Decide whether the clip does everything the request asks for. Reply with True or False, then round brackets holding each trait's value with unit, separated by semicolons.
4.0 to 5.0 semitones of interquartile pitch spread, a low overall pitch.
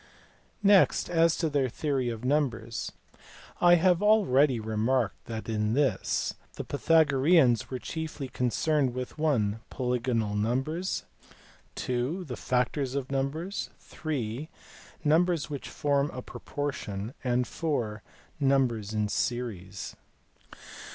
True (4.7 semitones; 130 Hz)